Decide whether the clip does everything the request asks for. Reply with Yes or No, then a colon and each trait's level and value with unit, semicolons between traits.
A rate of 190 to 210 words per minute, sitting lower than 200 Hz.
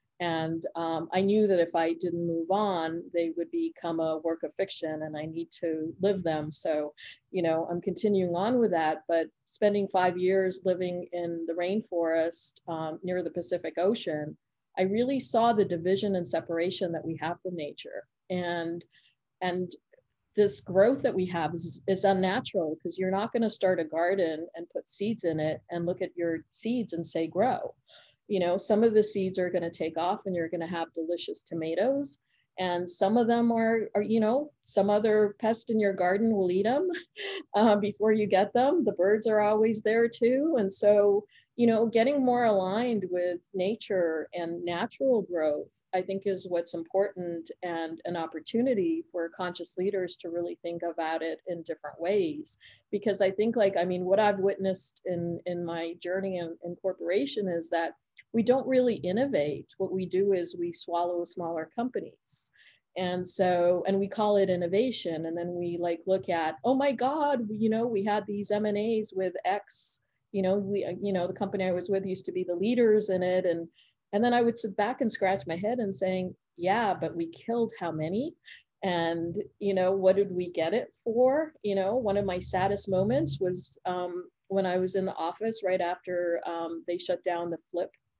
Yes: average, 195 wpm; medium, 185 Hz